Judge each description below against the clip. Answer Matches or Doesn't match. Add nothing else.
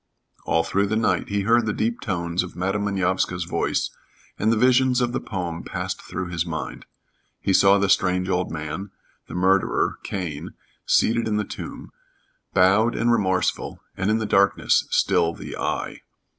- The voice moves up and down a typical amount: Matches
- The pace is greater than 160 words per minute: Matches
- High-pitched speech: Doesn't match